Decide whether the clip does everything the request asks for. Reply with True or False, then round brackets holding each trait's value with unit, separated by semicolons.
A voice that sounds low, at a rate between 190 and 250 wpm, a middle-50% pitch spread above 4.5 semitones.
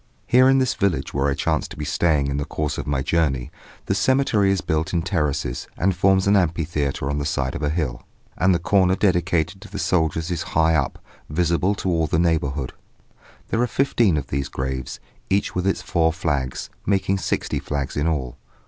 True (80 Hz; 200 wpm; 4.9 semitones)